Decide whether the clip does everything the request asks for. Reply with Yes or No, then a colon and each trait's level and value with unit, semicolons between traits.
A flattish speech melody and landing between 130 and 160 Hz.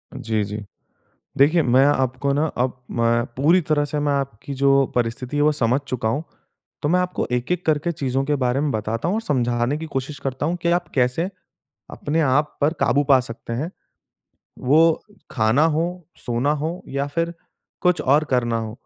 No: average, 3.8 semitones; medium, 140 Hz